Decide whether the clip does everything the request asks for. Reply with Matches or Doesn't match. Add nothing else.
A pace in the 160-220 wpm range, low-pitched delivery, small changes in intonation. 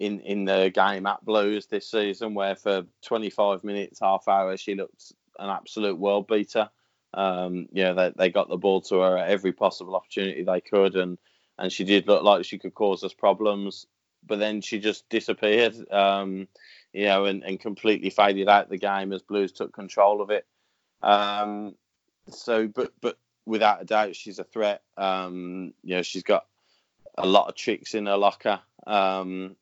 Matches